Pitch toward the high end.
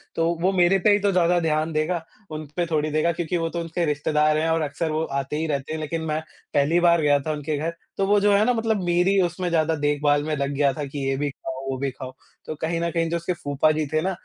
No: medium, 160 Hz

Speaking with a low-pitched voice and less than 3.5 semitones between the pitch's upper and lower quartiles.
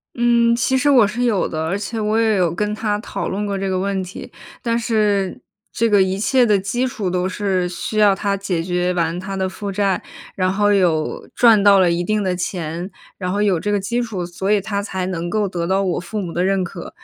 No: high, 195 Hz; narrow, 2.6 semitones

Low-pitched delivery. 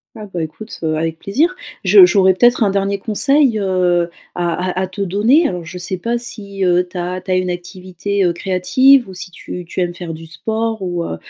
No: medium, 185 Hz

